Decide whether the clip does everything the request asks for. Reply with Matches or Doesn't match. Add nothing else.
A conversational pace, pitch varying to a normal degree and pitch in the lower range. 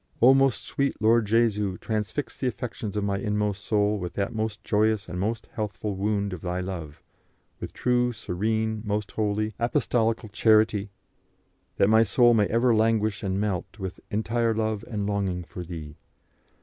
Doesn't match